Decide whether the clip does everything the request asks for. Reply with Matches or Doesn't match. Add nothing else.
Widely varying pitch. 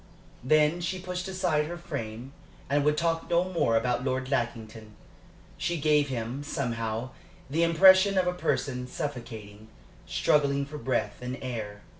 Matches